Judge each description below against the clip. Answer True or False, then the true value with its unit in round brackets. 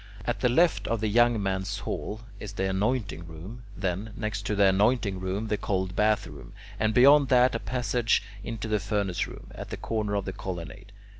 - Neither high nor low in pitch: False (105 Hz)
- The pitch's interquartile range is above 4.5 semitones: False (3.3 semitones)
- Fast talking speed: True (215 wpm)